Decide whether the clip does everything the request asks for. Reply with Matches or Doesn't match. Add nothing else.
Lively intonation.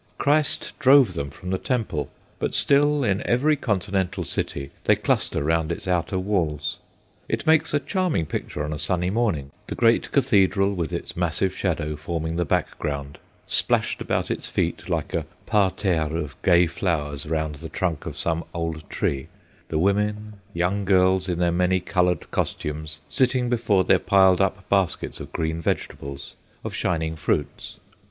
Doesn't match